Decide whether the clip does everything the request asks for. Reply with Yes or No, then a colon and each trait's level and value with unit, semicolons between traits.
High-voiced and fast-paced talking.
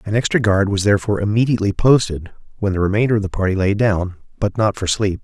No: low, 105 Hz; fast, 220 wpm